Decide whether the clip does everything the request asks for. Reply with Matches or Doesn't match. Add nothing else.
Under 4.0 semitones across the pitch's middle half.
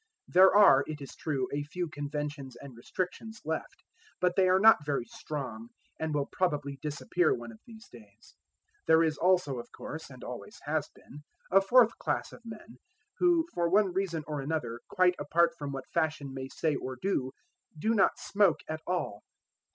Doesn't match